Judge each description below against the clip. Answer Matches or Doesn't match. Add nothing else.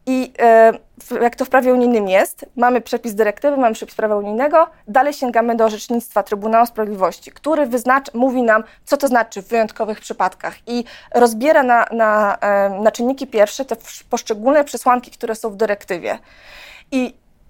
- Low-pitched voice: Doesn't match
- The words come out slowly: Doesn't match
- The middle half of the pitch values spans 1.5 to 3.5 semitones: Matches